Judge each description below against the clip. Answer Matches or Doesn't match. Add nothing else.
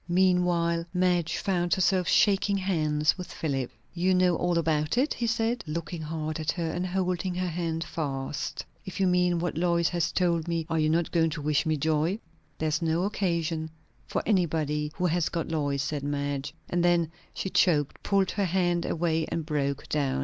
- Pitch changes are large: Doesn't match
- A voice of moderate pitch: Matches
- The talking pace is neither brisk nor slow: Matches